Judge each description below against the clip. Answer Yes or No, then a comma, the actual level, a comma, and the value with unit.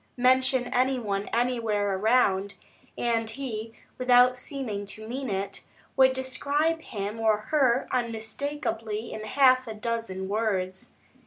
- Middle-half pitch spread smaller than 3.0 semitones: No, average, 3.5 semitones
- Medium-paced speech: No, slow, 125 wpm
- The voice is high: Yes, high, 230 Hz